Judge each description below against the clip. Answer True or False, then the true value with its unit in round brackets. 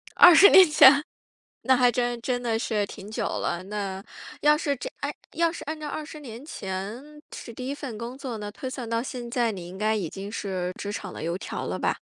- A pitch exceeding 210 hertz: True (235 Hz)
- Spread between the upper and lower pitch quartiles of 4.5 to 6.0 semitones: True (5.1 semitones)